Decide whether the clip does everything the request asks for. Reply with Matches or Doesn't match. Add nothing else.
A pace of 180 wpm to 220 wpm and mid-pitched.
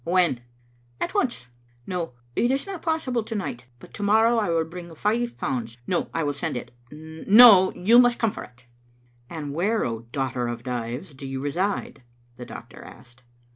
Matches